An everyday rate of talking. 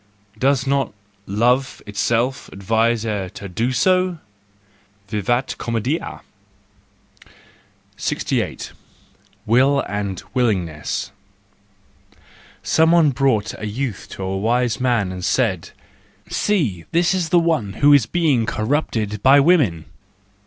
No: slow, 105 wpm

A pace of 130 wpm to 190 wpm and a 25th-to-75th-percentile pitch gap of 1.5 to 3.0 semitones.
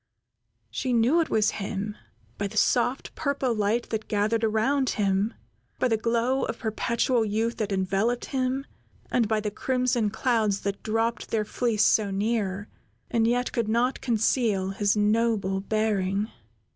Yes: average, 150 wpm; narrow, 2.5 semitones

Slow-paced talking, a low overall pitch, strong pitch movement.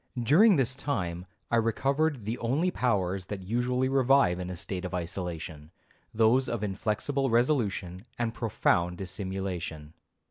Yes: slow, 130 wpm; low, 110 Hz; wide, 6.1 semitones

